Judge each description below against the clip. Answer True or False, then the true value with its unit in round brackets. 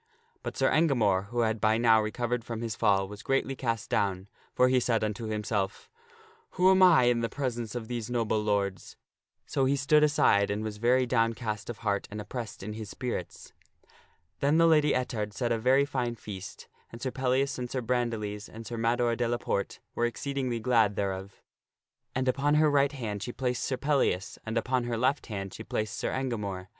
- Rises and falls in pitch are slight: False (3.4 semitones)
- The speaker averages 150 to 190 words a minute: False (200 wpm)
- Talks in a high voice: False (120 Hz)